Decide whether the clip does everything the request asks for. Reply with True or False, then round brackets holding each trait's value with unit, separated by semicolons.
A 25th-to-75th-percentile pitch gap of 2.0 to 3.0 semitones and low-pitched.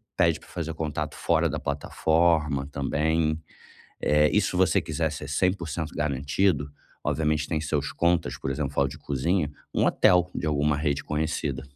True (2.4 semitones; 75 Hz)